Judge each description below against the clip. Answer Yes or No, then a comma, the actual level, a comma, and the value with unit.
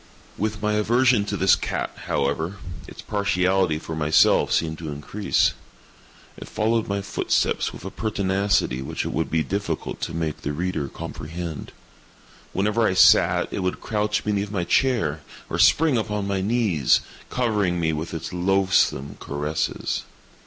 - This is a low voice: Yes, very low, 95 Hz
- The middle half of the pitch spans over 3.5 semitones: Yes, average, 4.7 semitones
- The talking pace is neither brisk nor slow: Yes, average, 150 wpm